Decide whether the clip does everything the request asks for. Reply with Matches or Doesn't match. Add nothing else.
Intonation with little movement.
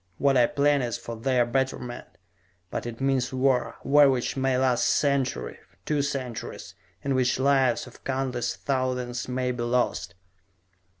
Matches